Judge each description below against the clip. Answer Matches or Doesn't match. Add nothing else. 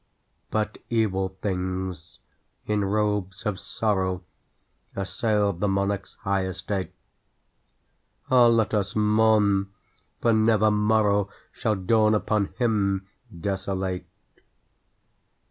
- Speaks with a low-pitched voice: Matches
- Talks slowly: Matches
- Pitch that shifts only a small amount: Matches